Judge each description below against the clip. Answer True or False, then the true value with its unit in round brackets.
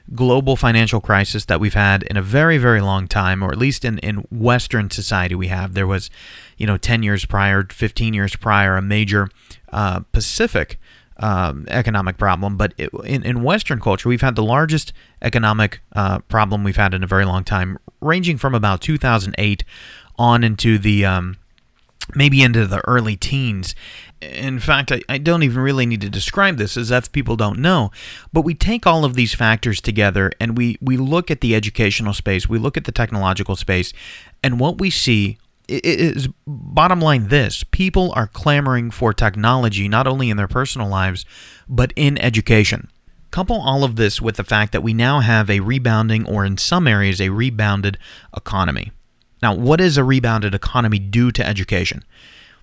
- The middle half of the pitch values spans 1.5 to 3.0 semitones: False (4.3 semitones)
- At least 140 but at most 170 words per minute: False (180 wpm)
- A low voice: True (110 Hz)